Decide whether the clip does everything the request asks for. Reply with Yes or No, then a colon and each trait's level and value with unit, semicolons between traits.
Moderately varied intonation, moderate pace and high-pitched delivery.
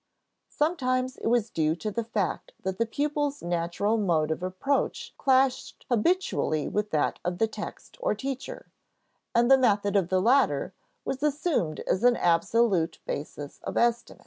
No: wide, 6.5 semitones; average, 155 wpm; high, 225 Hz